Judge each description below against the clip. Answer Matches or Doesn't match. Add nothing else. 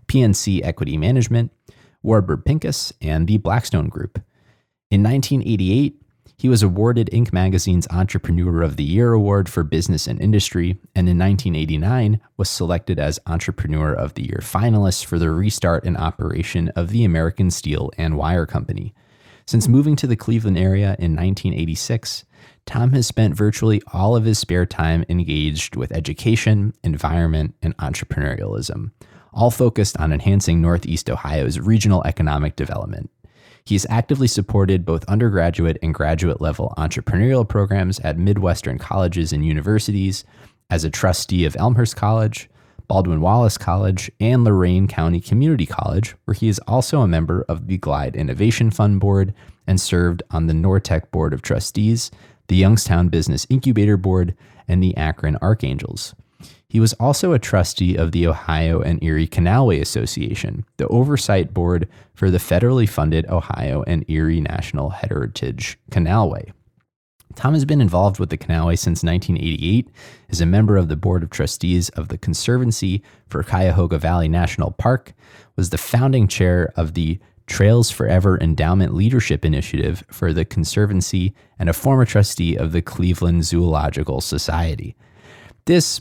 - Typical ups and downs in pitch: Matches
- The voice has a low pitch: Matches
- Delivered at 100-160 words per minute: Matches